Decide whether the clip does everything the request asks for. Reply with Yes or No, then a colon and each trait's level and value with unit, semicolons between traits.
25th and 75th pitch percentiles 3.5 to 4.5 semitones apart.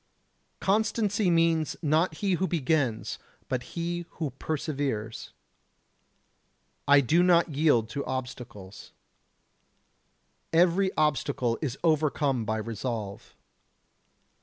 No: average, 5.3 semitones